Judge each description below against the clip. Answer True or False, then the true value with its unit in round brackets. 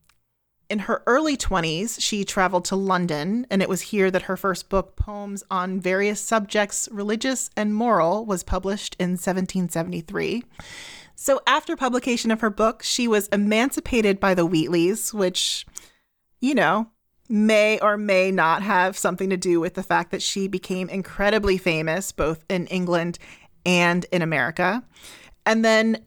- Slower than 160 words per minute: True (150 wpm)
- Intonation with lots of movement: False (3.0 semitones)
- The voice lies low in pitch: False (195 Hz)